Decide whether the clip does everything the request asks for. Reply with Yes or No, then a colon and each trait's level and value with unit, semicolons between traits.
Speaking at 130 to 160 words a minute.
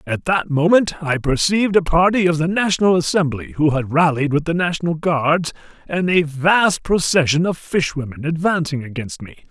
No: average, 170 wpm